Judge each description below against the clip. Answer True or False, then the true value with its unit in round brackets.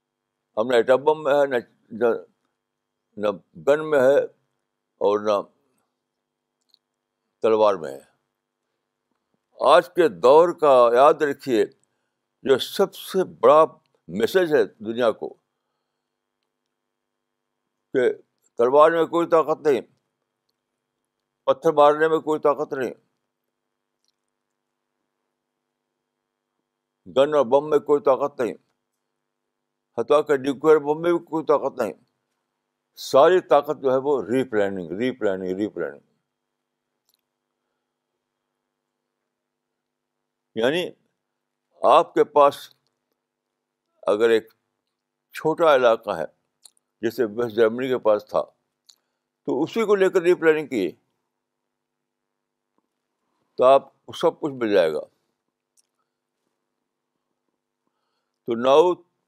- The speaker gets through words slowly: True (100 wpm)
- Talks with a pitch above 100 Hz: True (140 Hz)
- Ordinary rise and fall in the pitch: False (6.0 semitones)